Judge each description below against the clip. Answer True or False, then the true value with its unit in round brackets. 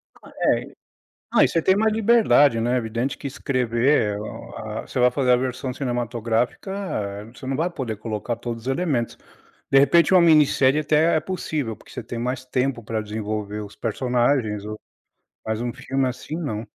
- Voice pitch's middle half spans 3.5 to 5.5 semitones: True (4.3 semitones)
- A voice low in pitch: True (125 Hz)